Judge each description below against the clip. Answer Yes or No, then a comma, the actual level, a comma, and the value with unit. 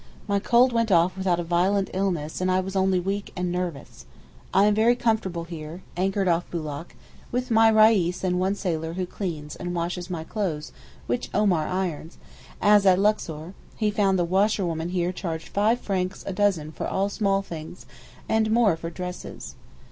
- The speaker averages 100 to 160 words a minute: No, average, 180 wpm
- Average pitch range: Yes, average, 3.0 semitones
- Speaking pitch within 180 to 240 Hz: Yes, medium, 185 Hz